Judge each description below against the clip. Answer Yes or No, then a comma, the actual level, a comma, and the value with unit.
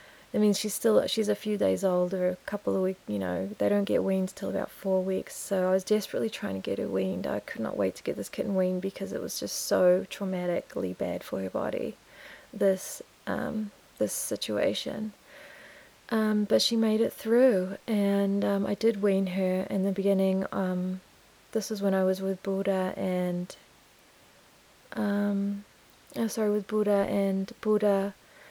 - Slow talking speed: No, average, 185 wpm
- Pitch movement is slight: Yes, narrow, 2.1 semitones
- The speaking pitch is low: No, high, 195 Hz